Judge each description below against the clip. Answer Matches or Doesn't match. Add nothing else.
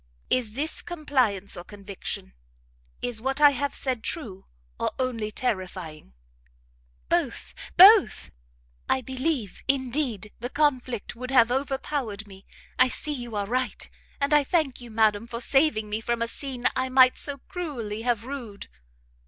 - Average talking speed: Matches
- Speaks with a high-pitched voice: Matches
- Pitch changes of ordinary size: Matches